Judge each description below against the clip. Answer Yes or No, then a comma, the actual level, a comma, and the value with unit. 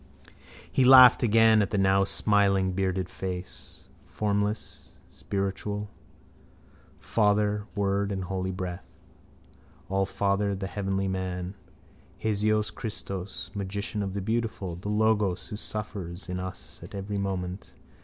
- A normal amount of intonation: No, narrow, 1.7 semitones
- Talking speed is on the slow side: Yes, slow, 115 wpm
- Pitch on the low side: Yes, low, 100 Hz